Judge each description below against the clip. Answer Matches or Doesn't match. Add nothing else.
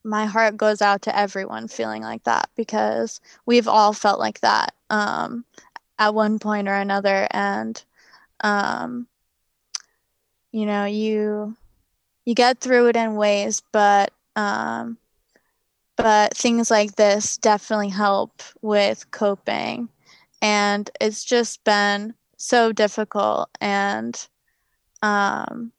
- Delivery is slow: Matches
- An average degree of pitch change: Doesn't match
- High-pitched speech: Matches